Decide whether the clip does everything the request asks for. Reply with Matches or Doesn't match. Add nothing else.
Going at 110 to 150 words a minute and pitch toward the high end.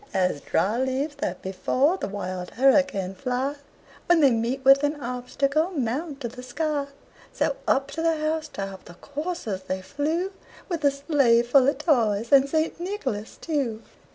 Doesn't match